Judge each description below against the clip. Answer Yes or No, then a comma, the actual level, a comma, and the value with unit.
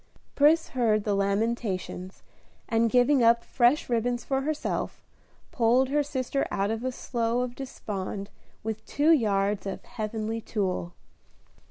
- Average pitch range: Yes, average, 3.7 semitones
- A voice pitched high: Yes, high, 230 Hz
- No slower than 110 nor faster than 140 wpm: Yes, slow, 135 wpm